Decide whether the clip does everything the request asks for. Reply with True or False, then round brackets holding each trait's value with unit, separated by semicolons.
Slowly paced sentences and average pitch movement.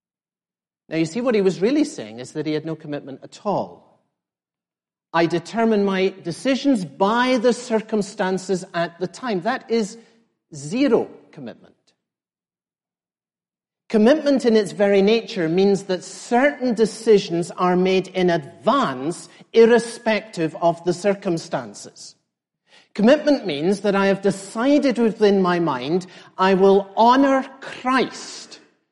True (125 wpm; 4.4 semitones)